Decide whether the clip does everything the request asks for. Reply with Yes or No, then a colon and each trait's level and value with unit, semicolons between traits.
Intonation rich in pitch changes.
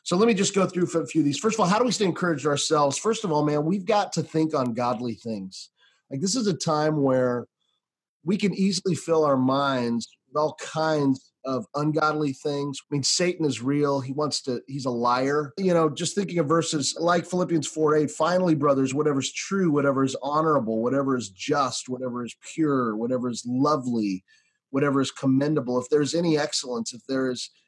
No: average, 4.0 semitones